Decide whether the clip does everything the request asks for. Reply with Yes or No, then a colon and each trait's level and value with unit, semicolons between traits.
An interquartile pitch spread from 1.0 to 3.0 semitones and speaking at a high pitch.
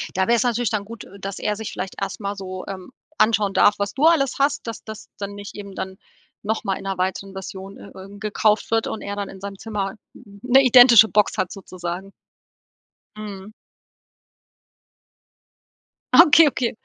Yes: narrow, 2.5 semitones; high, 205 Hz